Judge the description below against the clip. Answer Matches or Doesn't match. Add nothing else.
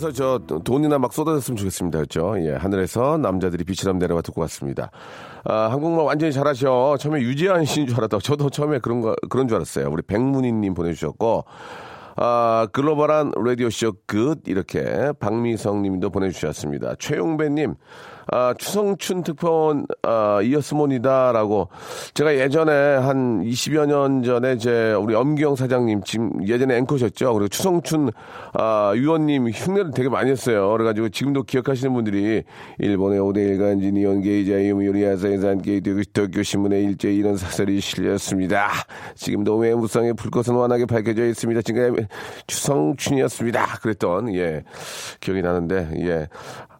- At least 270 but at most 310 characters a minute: Doesn't match